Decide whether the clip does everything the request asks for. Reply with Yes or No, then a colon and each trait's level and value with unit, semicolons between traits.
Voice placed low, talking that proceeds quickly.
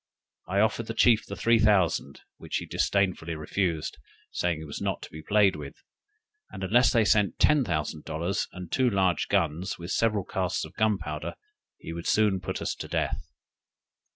No: very low, 95 Hz; average, 180 wpm